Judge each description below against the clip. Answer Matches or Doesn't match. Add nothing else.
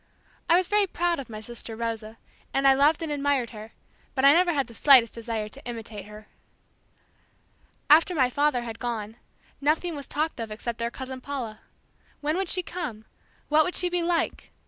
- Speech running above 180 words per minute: Matches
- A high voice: Matches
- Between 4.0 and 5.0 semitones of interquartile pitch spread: Doesn't match